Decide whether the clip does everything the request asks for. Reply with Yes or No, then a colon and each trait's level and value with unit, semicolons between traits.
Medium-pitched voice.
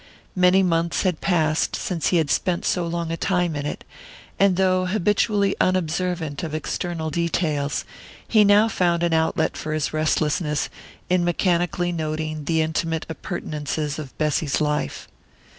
Yes: medium, 165 Hz